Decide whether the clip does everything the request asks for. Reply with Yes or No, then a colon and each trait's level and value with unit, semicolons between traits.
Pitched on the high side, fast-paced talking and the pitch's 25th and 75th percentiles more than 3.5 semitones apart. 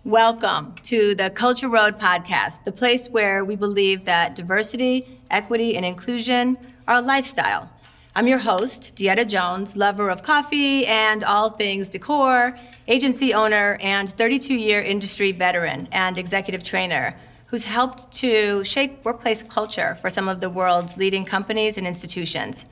No: high, 215 Hz; average, 145 wpm; average, 4.1 semitones